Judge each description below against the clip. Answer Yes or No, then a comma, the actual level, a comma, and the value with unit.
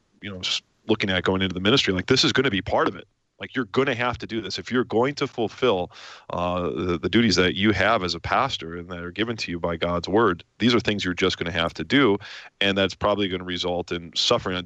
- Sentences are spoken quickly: Yes, fast, 280 wpm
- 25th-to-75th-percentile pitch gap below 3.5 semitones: No, average, 4.4 semitones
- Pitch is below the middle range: Yes, very low, 95 Hz